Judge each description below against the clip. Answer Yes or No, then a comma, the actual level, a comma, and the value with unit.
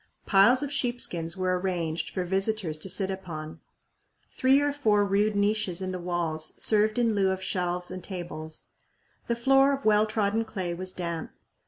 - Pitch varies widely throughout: No, average, 3.6 semitones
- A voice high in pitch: Yes, high, 195 Hz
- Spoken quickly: No, average, 175 wpm